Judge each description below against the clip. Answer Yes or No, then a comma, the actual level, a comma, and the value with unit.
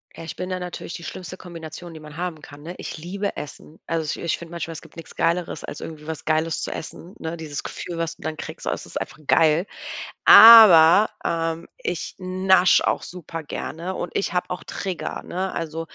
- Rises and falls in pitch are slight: Yes, narrow, 2.2 semitones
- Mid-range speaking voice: Yes, medium, 165 Hz